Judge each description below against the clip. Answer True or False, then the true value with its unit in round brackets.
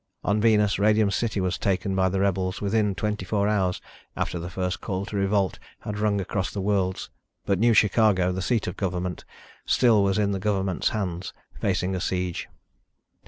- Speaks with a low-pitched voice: True (100 Hz)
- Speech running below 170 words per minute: False (180 wpm)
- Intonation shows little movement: True (2.2 semitones)